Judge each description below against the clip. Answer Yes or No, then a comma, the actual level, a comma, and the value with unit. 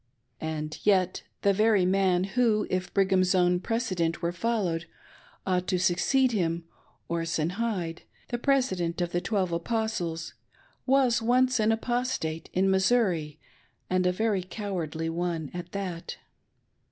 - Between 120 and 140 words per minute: Yes, slow, 135 wpm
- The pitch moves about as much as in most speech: Yes, average, 4.4 semitones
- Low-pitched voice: No, medium, 185 Hz